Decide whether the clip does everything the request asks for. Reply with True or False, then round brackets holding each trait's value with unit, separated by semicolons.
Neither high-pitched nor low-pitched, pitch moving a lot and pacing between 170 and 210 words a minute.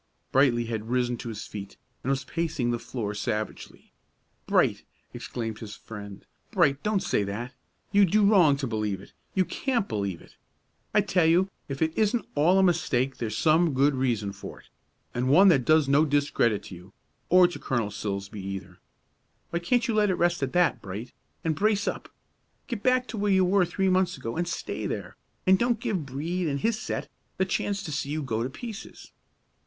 True (145 Hz; 8.5 semitones; 195 wpm)